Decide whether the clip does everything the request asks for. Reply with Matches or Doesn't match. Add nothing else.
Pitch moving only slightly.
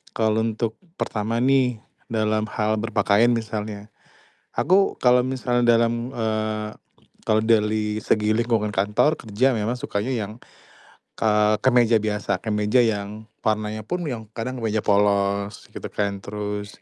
Matches